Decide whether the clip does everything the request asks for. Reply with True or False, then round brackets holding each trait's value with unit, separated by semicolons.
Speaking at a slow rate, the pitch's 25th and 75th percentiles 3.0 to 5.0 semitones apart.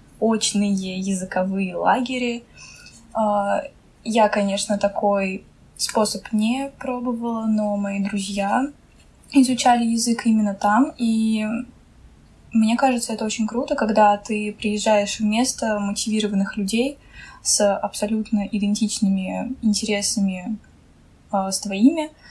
False (95 wpm; 2.5 semitones)